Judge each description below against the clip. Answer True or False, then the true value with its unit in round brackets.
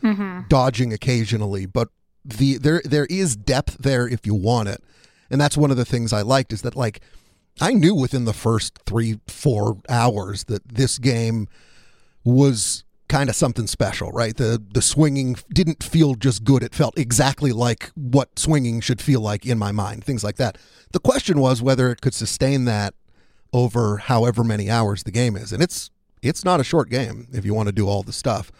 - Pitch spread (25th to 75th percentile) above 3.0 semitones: True (4.0 semitones)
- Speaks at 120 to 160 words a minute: False (195 wpm)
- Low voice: True (120 Hz)